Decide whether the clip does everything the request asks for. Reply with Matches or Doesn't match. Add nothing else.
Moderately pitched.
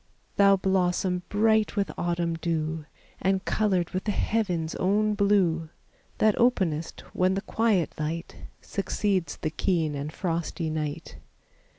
Matches